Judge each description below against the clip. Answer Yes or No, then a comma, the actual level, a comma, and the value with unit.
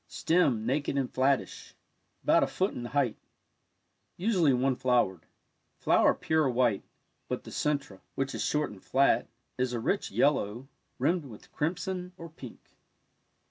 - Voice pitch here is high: No, low, 135 Hz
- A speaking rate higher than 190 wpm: No, average, 160 wpm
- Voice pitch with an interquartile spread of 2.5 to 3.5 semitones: No, average, 4.4 semitones